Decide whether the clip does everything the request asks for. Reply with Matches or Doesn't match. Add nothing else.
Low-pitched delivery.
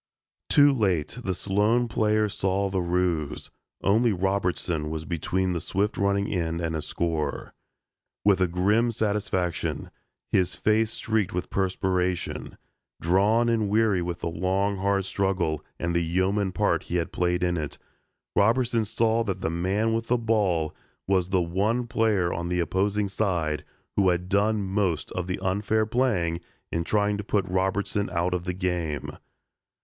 Matches